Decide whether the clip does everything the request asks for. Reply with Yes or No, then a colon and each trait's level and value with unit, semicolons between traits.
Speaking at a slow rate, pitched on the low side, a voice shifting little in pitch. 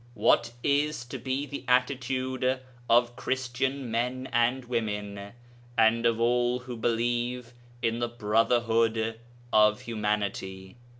Yes: slow, 115 wpm; low, 120 Hz; narrow, 2.0 semitones